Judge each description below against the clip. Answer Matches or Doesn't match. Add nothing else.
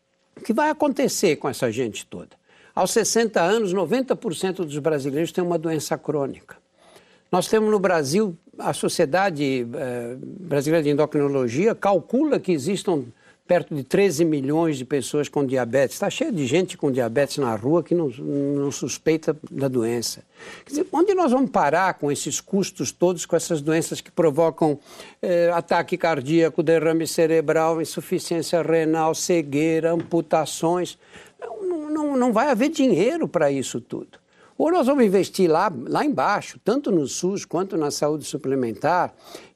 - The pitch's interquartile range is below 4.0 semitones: Doesn't match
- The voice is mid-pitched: Matches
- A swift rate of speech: Doesn't match